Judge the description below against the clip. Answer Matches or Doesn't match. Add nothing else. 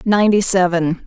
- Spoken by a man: Doesn't match